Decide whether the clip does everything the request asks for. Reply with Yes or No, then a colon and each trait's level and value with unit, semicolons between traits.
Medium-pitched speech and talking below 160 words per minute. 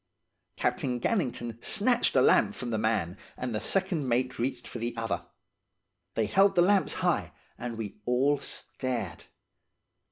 No: low, 120 Hz; average, 150 wpm